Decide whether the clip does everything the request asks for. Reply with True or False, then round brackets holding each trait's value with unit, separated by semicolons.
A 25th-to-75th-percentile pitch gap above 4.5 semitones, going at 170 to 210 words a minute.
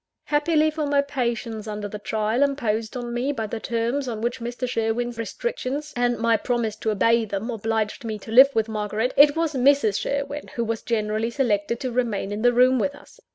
False (3.6 semitones; 200 wpm)